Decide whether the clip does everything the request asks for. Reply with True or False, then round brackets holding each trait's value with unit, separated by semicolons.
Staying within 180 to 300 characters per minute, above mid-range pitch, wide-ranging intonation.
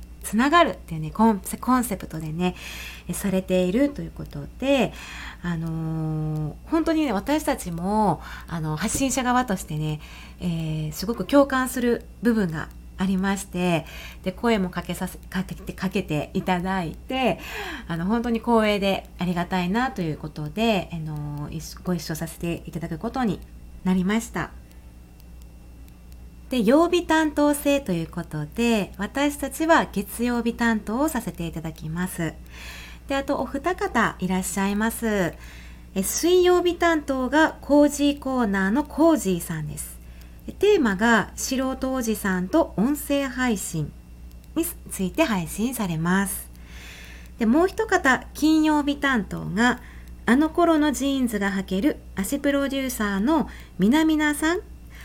True (280 characters per minute; 200 Hz; 8.3 semitones)